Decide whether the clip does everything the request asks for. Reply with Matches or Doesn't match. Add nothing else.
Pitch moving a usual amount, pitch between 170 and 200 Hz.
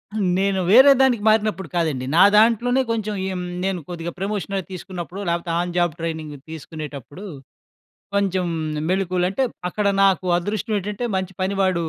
Matches